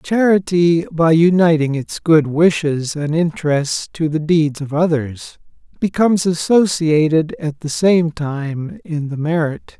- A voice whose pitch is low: No, medium, 160 Hz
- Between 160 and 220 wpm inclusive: No, slow, 135 wpm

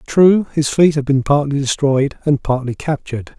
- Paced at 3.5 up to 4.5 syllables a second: No, 4.7 syllables/s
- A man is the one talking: Yes, male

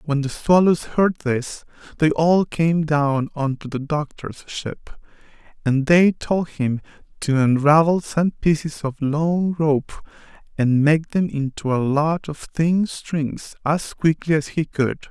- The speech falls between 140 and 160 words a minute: Yes, average, 155 wpm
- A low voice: No, medium, 150 Hz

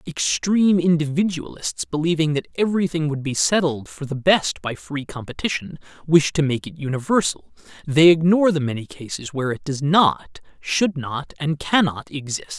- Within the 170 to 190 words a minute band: No, average, 155 wpm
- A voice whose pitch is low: No, medium, 155 Hz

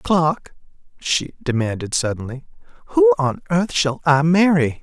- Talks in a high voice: No, medium, 140 Hz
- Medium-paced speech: No, slow, 125 wpm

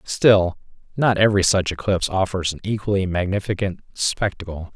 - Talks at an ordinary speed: No, slow, 125 wpm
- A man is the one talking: Yes, male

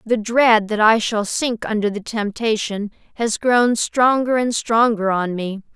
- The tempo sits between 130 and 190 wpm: Yes, average, 165 wpm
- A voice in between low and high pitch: No, high, 220 Hz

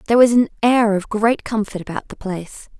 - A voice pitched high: Yes, high, 215 Hz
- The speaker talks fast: Yes, fast, 215 wpm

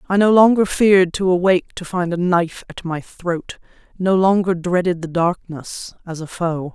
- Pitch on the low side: No, medium, 180 Hz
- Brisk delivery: No, average, 185 wpm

